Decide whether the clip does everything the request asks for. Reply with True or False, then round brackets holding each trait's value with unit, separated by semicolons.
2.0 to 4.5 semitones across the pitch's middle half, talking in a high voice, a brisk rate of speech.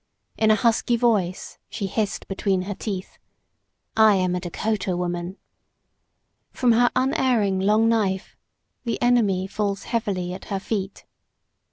False (3.2 semitones; 205 Hz; 135 wpm)